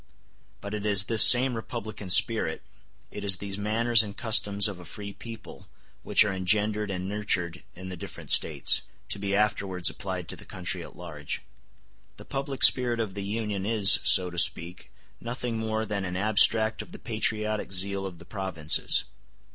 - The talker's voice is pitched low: Yes, low, 100 Hz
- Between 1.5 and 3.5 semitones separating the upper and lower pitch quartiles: Yes, average, 2.7 semitones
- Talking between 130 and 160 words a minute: No, average, 175 wpm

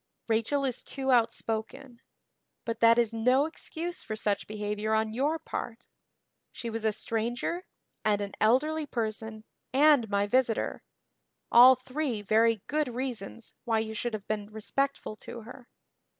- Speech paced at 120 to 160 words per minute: Yes, average, 145 wpm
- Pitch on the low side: No, high, 230 Hz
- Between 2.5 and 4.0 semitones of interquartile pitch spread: Yes, average, 3.2 semitones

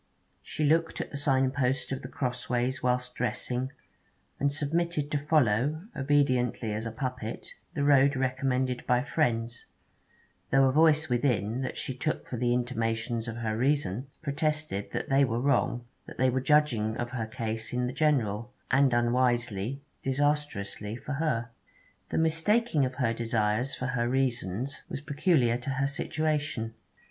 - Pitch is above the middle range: No, low, 130 Hz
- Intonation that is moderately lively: Yes, average, 3.3 semitones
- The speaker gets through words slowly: No, average, 155 wpm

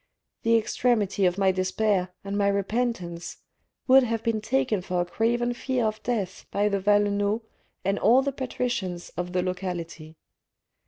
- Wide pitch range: No, average, 4.0 semitones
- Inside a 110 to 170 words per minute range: Yes, average, 155 wpm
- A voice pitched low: No, high, 205 Hz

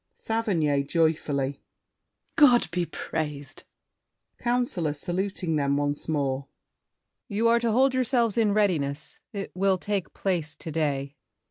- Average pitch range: No, wide, 6.7 semitones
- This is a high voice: No, medium, 170 Hz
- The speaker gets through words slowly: Yes, slow, 120 wpm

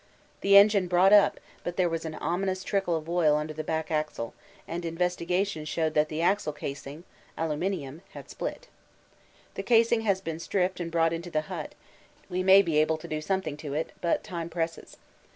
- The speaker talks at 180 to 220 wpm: Yes, average, 190 wpm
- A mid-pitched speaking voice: Yes, medium, 170 Hz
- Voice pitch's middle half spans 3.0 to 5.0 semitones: Yes, average, 3.3 semitones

